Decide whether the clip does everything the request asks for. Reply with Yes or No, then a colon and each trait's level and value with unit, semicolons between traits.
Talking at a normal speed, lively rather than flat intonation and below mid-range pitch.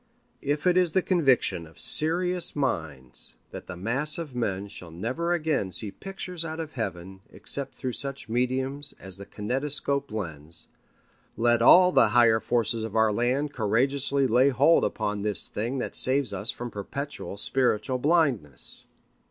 Yes: average, 155 wpm; wide, 5.8 semitones; low, 125 Hz